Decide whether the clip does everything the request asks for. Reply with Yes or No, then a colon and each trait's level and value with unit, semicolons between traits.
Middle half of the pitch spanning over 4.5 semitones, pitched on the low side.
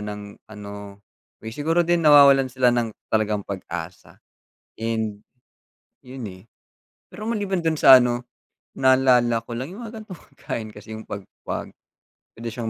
Yes: average, 5.2 semitones; low, 120 Hz